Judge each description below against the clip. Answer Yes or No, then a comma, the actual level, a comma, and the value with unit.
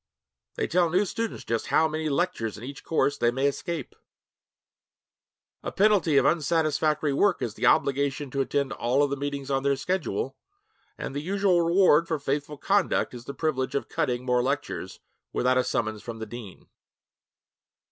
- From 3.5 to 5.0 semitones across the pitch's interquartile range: Yes, average, 4.1 semitones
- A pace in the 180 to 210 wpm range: No, average, 165 wpm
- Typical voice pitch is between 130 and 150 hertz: Yes, medium, 140 Hz